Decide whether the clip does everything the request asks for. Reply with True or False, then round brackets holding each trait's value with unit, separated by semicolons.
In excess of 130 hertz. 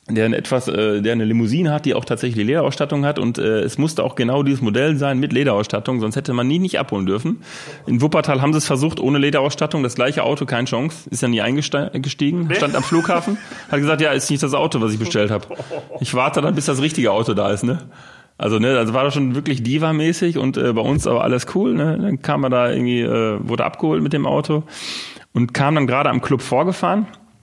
True (140 Hz)